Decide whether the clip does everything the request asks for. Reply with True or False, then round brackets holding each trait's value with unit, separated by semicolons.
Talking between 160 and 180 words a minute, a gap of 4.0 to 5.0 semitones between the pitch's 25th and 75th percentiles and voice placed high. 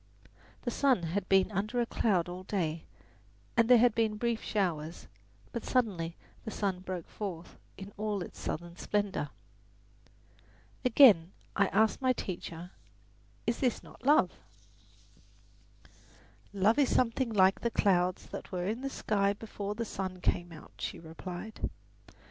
False (145 wpm; 4.3 semitones; 200 Hz)